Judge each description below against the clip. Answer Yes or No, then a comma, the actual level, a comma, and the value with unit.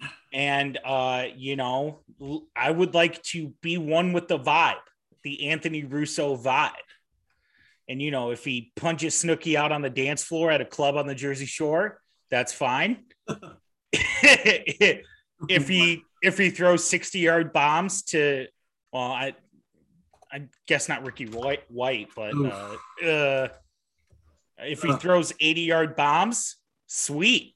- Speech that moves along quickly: No, average, 140 wpm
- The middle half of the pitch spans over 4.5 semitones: No, average, 3.4 semitones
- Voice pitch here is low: No, medium, 150 Hz